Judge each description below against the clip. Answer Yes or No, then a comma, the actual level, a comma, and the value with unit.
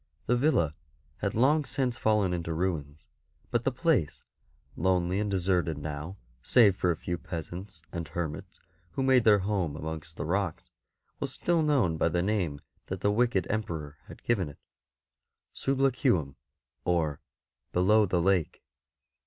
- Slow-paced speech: No, average, 155 wpm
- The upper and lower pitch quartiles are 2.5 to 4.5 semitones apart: No, average, 5.2 semitones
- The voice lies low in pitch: Yes, very low, 90 Hz